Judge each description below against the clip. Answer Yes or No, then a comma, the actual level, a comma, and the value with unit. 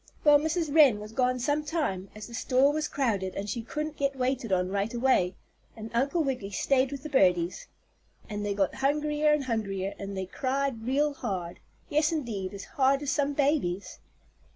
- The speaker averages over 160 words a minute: Yes, average, 185 wpm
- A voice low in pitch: No, very high, 255 Hz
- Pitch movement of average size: No, wide, 6.3 semitones